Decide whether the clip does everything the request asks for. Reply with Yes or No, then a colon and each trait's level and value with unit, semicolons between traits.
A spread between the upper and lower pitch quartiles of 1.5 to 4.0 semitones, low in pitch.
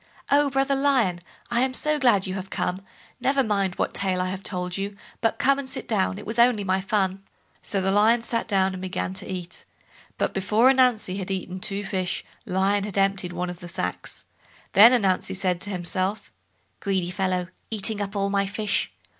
No: average, 3.2 semitones; high, 195 Hz